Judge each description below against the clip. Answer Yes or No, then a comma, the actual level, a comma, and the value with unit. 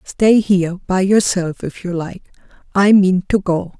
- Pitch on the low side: No, high, 190 Hz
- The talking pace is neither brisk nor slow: Yes, average, 175 wpm